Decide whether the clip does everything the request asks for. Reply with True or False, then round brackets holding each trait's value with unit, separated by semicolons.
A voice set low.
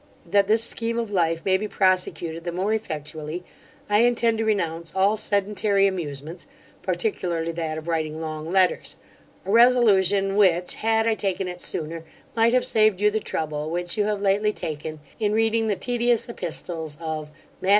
False (190 Hz)